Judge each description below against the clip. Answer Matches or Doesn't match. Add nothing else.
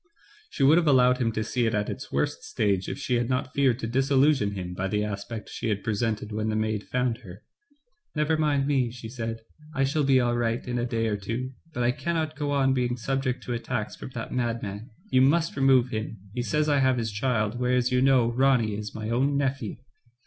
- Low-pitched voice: Matches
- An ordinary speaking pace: Doesn't match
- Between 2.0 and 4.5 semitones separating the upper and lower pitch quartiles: Matches